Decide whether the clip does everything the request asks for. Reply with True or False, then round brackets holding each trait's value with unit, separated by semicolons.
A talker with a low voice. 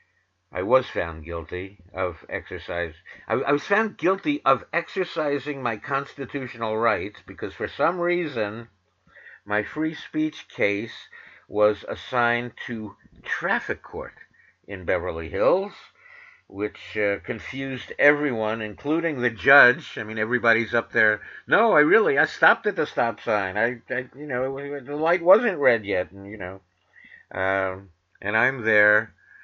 True (120 Hz)